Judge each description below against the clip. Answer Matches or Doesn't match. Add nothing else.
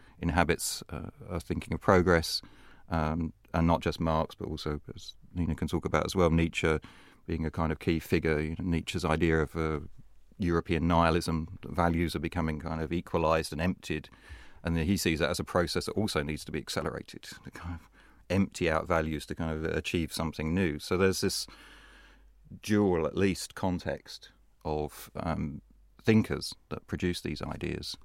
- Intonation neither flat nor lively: Doesn't match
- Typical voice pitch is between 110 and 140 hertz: Doesn't match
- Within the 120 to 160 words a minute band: Doesn't match